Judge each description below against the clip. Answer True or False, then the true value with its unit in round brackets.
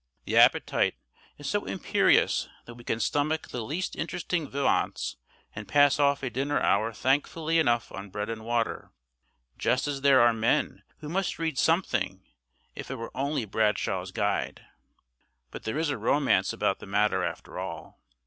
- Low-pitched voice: True (130 Hz)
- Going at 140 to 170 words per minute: True (165 wpm)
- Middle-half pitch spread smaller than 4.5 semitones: False (4.9 semitones)